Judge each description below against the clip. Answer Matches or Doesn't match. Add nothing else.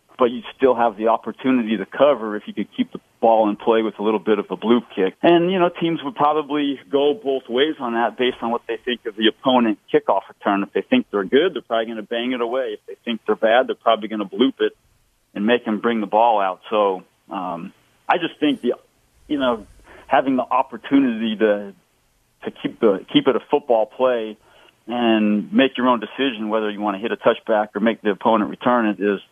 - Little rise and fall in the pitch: Doesn't match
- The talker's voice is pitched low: Matches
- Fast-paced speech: Matches